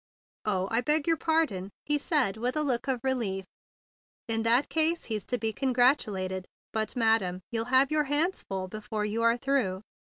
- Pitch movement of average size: Yes, average, 4.8 semitones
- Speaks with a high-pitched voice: Yes, high, 235 Hz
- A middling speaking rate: Yes, average, 180 wpm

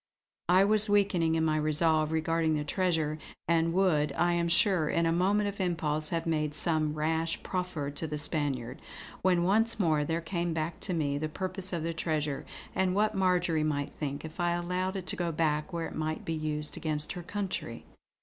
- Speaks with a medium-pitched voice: Yes, medium, 165 Hz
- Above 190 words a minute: Yes, average, 200 wpm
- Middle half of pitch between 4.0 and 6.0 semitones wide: No, average, 2.8 semitones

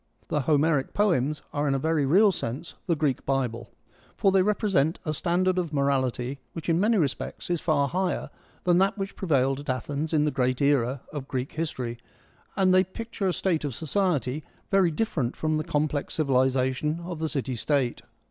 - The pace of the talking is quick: No, average, 185 wpm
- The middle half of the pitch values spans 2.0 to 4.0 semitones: No, average, 4.7 semitones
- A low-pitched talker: No, medium, 150 Hz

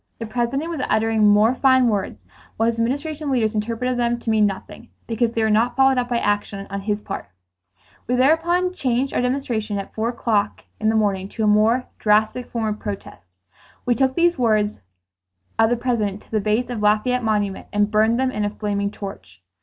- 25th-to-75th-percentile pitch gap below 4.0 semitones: Yes, average, 3.1 semitones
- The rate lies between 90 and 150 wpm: No, average, 190 wpm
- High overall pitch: Yes, high, 225 Hz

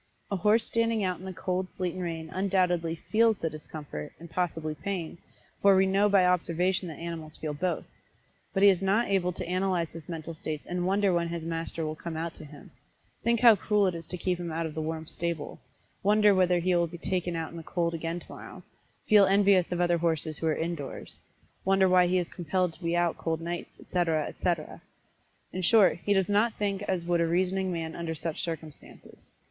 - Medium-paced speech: No, fast, 215 wpm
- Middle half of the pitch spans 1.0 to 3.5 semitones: Yes, narrow, 2.6 semitones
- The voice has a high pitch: No, medium, 175 Hz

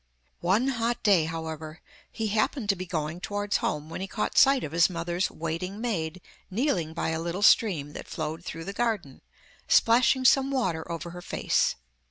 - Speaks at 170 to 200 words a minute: Yes, average, 180 wpm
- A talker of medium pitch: Yes, medium, 180 Hz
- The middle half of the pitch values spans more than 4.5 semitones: Yes, average, 5.3 semitones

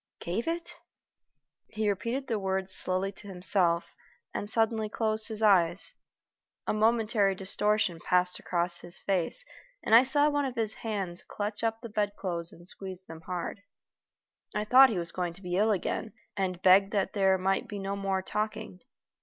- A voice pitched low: No, high, 200 Hz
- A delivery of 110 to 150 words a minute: No, average, 170 wpm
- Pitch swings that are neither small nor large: Yes, average, 3.1 semitones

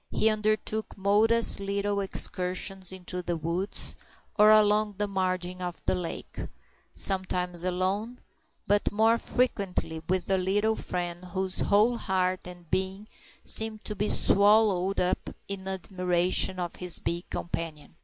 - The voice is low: No, high, 190 Hz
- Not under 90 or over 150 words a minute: Yes, slow, 135 wpm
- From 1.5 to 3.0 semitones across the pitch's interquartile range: Yes, narrow, 2.5 semitones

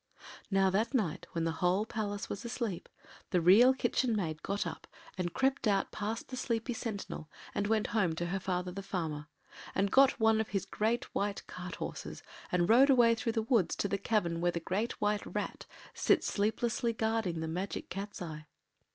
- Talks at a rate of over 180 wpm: Yes, average, 190 wpm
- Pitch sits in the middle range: No, high, 205 Hz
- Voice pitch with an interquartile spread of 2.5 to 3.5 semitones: No, average, 4.0 semitones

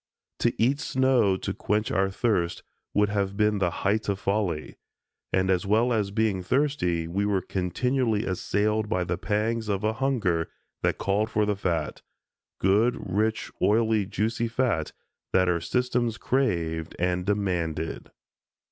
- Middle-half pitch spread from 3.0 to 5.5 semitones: Yes, average, 3.4 semitones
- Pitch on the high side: No, low, 105 Hz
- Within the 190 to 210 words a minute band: No, average, 145 wpm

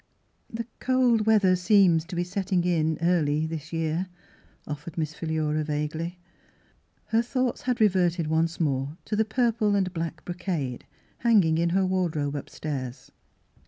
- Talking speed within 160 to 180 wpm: No, average, 145 wpm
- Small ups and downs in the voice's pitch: No, average, 4.2 semitones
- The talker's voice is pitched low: No, medium, 170 Hz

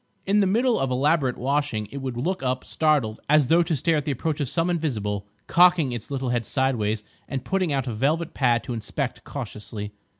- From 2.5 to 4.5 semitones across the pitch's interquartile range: No, average, 5.0 semitones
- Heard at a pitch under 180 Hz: Yes, low, 135 Hz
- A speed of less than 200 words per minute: No, fast, 205 wpm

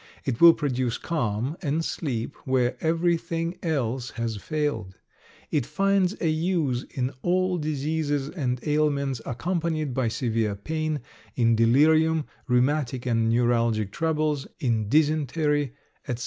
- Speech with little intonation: No, average, 4.7 semitones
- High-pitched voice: No, medium, 145 Hz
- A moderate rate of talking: No, slow, 120 wpm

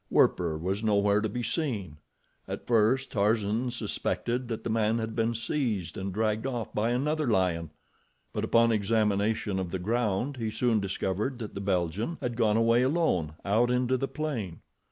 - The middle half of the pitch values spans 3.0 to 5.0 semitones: Yes, average, 3.4 semitones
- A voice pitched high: No, low, 110 Hz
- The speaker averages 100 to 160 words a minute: No, average, 170 wpm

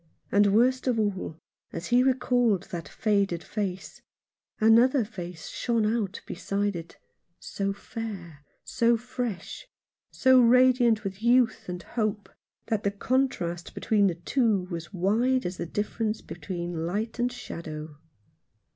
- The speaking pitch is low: No, high, 210 Hz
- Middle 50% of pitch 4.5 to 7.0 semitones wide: Yes, average, 5.0 semitones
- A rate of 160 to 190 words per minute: No, average, 145 wpm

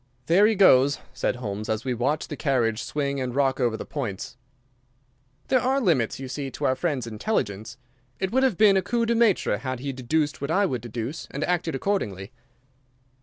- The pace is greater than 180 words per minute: Yes, average, 195 wpm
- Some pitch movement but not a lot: No, wide, 7.2 semitones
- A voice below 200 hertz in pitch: Yes, medium, 140 Hz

